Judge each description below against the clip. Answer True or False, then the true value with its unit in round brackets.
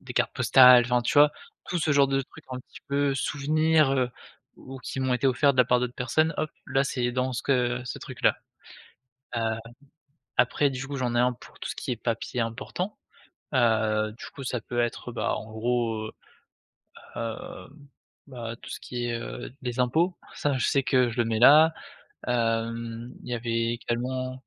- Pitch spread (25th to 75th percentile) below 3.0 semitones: True (2.5 semitones)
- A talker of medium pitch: False (125 Hz)